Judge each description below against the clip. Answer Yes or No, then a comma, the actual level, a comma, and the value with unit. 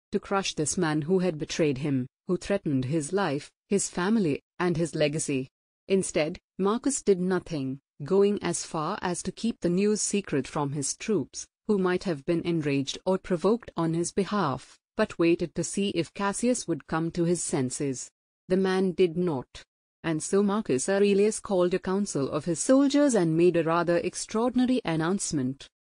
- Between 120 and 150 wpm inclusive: No, average, 170 wpm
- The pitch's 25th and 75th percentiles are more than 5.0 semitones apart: No, average, 3.9 semitones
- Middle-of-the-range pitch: Yes, medium, 180 Hz